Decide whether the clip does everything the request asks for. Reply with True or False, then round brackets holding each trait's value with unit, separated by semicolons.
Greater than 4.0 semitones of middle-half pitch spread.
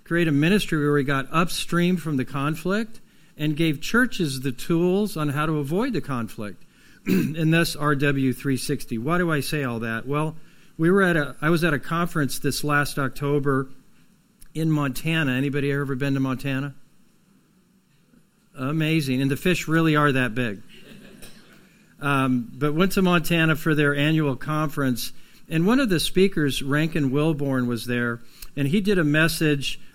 False (3.7 semitones)